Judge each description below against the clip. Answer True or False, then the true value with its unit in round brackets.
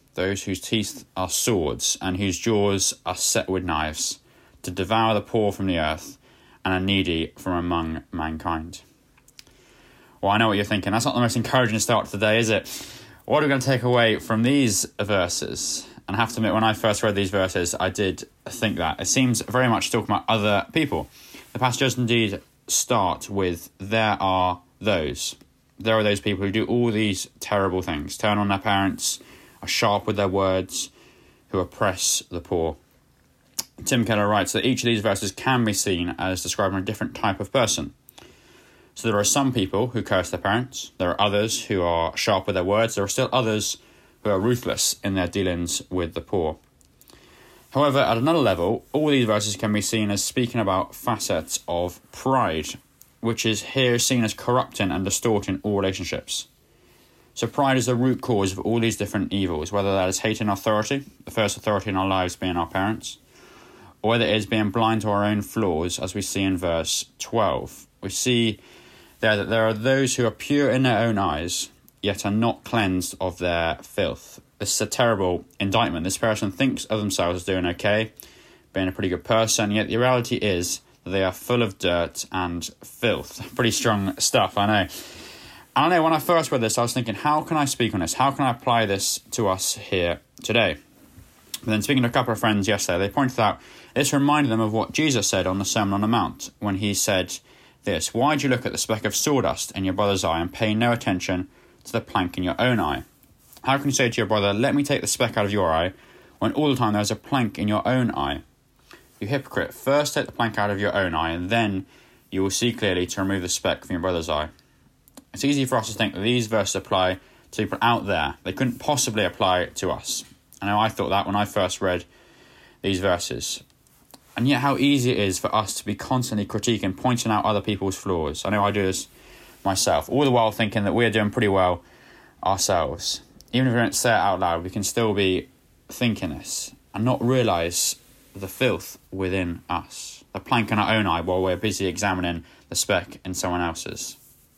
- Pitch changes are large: False (3.8 semitones)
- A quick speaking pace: True (210 wpm)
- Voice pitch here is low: True (105 Hz)